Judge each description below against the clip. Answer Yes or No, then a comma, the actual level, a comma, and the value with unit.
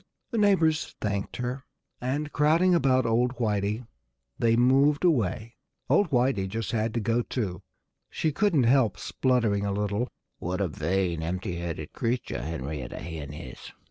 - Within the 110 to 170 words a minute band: Yes, average, 145 wpm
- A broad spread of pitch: Yes, wide, 5.8 semitones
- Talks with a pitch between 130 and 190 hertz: No, low, 115 Hz